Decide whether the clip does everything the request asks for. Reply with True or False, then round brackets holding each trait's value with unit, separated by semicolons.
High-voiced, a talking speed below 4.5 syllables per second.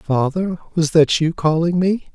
False (165 Hz; 4.1 syllables/s)